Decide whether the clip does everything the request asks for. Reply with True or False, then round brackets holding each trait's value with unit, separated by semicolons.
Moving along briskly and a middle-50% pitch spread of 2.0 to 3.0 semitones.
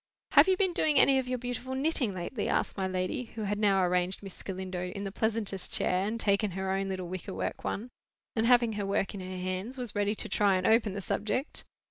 False (230 wpm; 4.1 semitones)